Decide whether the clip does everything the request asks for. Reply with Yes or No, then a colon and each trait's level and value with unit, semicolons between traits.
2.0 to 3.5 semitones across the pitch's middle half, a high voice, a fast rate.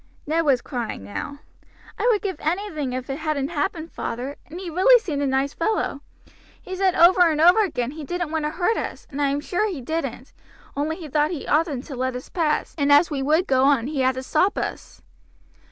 No: average, 4.3 semitones; very high, 300 Hz; fast, 220 wpm